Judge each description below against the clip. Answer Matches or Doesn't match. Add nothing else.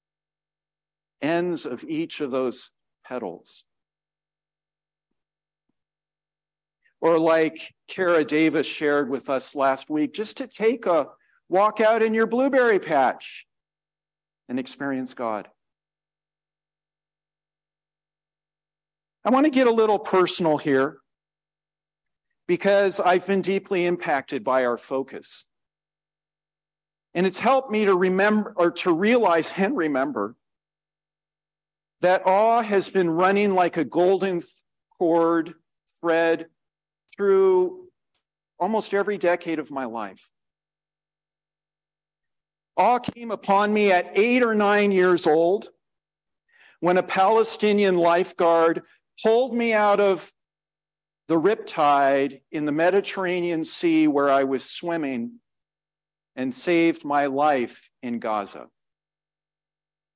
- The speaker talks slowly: Matches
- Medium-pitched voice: Matches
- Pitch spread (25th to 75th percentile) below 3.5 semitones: Doesn't match